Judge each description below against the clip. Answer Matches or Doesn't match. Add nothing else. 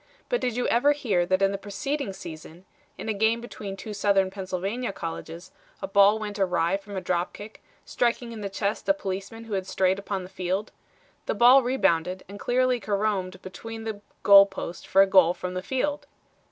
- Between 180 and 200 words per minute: Matches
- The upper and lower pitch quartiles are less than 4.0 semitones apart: Matches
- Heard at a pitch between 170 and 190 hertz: Doesn't match